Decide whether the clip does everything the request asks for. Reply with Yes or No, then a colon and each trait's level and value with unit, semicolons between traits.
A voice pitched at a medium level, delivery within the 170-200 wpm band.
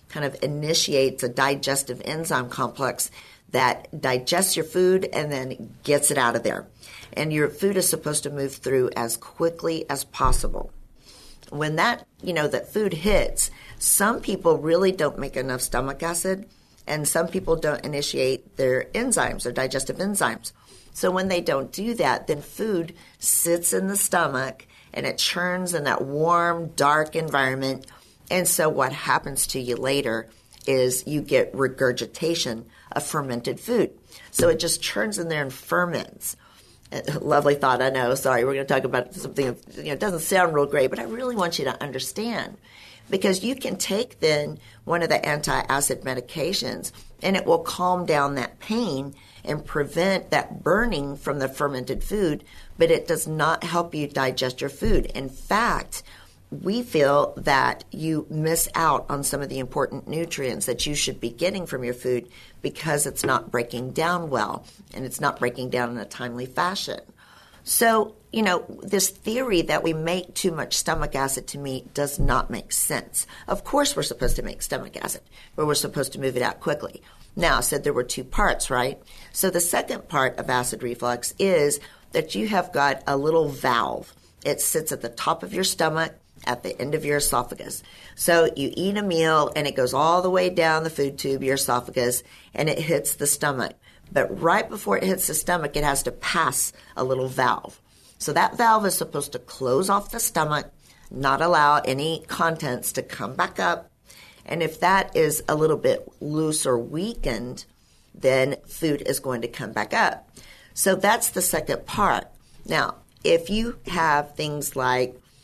Yes: medium, 150 Hz; average, 180 wpm